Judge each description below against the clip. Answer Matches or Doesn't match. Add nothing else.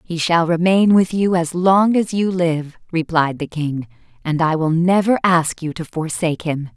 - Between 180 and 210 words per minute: Matches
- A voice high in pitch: Doesn't match